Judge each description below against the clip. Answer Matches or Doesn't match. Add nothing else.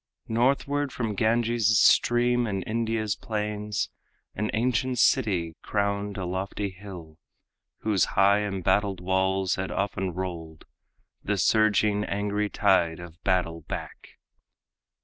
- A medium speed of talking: Doesn't match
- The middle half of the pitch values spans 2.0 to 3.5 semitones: Matches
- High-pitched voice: Doesn't match